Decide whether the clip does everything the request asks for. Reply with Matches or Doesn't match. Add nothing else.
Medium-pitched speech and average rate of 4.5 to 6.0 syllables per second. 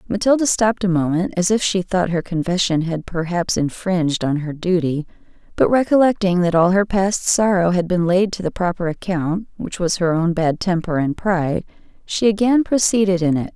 Matches